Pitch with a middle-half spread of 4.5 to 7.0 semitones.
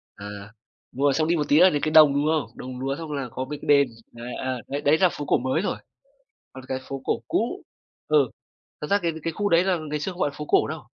No: average, 3.5 semitones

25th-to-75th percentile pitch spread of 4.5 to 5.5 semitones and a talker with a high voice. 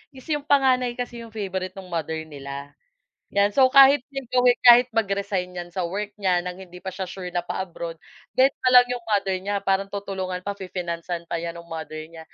Yes: average, 5.1 semitones; high, 195 Hz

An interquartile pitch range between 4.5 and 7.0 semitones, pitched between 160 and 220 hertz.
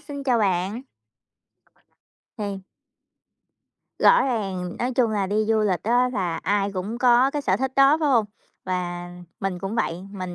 Yes: average, 5.1 semitones; high, 210 Hz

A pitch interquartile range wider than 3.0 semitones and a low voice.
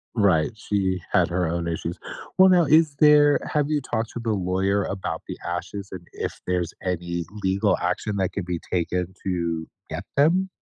Yes: average, 5.0 semitones; very low, 95 Hz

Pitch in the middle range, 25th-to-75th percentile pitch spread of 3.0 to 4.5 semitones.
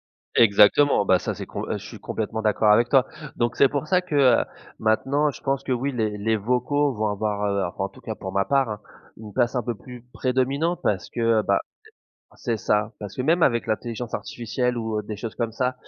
No: low, 115 Hz; average, 3.8 semitones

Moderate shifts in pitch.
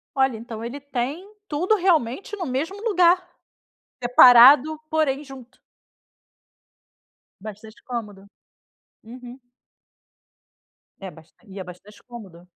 No: wide, 6.0 semitones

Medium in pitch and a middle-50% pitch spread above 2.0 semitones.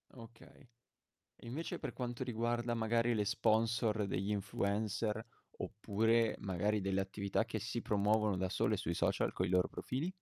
No: low, 110 Hz; average, 2.7 semitones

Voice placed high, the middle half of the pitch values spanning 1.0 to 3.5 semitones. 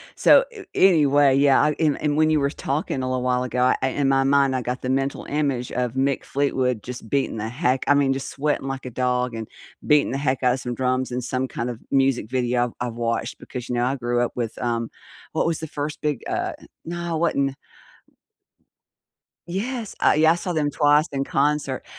No: low, 135 Hz; average, 2.7 semitones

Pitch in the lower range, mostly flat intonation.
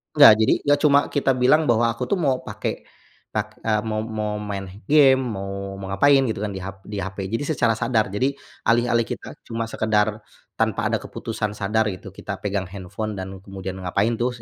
No: low, 110 Hz; average, 3.3 semitones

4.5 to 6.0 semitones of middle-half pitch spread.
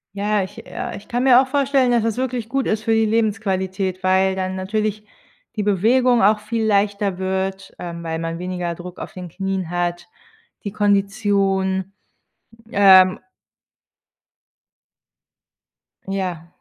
No: average, 2.8 semitones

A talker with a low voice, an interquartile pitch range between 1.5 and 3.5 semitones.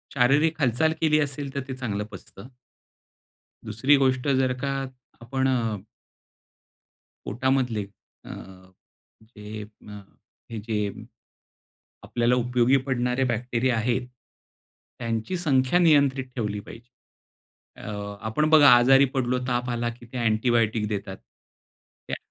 Yes: low, 125 Hz; average, 2.9 semitones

